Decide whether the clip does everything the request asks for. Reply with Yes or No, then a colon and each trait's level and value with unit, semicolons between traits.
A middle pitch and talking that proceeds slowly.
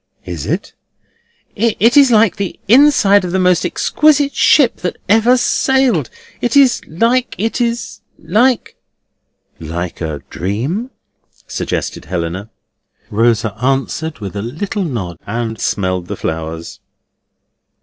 Yes: medium, 175 Hz; slow, 120 wpm